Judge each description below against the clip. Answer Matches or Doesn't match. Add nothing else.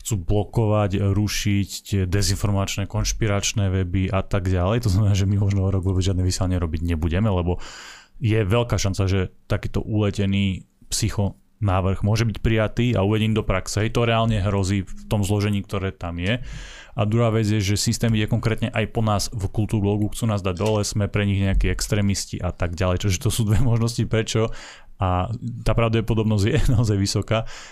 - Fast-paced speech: Matches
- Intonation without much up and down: Matches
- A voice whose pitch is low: Matches